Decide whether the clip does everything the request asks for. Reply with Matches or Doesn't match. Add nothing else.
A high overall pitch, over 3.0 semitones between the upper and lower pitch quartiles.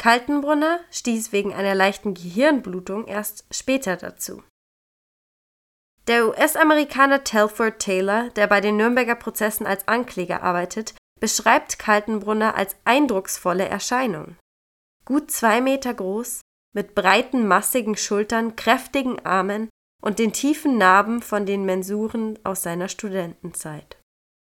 Matches